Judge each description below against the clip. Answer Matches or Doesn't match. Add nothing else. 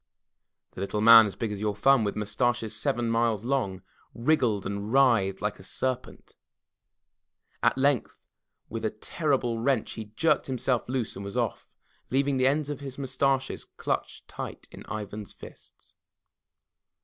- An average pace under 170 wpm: Matches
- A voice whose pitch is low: Matches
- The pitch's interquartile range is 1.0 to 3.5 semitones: Doesn't match